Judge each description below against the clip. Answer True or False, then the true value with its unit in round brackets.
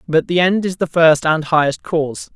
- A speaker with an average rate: False (230 wpm)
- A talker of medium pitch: True (165 Hz)